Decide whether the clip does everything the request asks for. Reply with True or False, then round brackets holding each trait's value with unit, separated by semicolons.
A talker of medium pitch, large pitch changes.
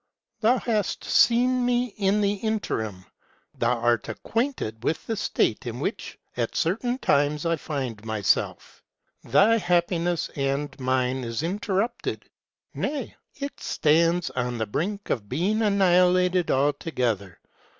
True (175 Hz; 8.5 semitones)